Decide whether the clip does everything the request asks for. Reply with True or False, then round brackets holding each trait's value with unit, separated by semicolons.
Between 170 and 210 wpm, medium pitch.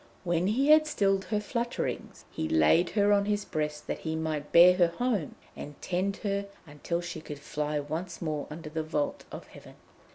True (190 wpm; 170 Hz)